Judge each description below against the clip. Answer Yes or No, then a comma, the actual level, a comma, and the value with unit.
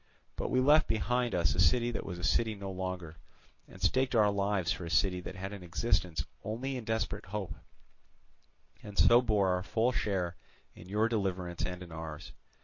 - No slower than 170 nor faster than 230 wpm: Yes, average, 190 wpm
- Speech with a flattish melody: No, average, 3.9 semitones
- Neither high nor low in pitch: No, low, 100 Hz